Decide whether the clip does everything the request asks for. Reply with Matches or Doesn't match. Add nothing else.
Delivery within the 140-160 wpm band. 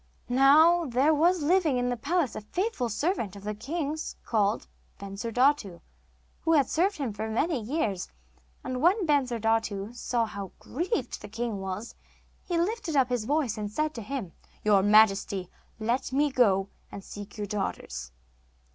Matches